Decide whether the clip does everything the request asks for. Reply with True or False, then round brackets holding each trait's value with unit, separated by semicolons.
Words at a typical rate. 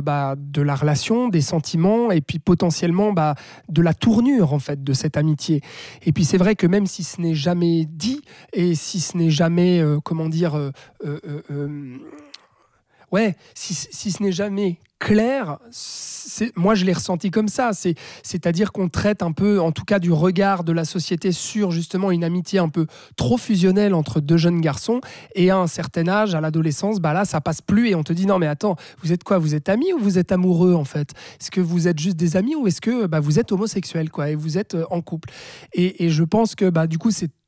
False (225 wpm)